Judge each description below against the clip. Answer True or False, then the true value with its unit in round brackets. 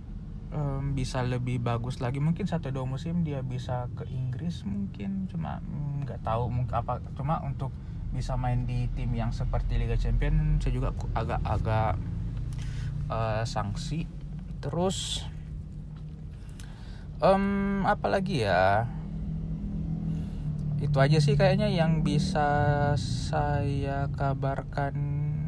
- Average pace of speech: True (110 wpm)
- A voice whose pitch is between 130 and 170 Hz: True (135 Hz)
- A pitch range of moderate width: True (4.2 semitones)